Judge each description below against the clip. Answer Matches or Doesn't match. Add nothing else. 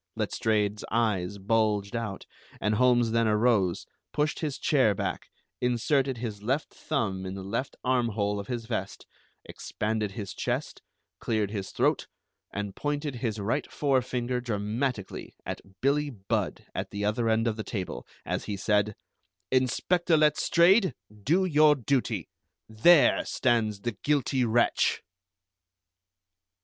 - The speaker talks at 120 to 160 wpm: Matches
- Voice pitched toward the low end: Matches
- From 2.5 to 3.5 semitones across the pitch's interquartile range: Doesn't match